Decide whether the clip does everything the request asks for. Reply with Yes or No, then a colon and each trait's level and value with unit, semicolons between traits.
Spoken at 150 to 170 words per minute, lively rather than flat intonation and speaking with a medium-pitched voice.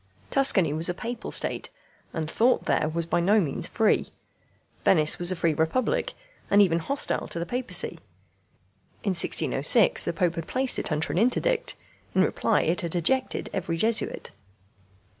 Yes: average, 165 wpm; wide, 6.2 semitones; medium, 180 Hz